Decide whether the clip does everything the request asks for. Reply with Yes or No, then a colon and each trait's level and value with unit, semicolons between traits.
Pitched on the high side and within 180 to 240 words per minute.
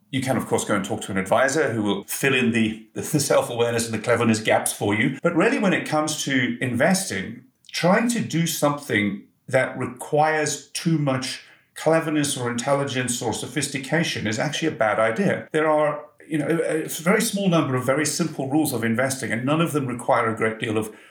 No: medium, 140 Hz; average, 200 wpm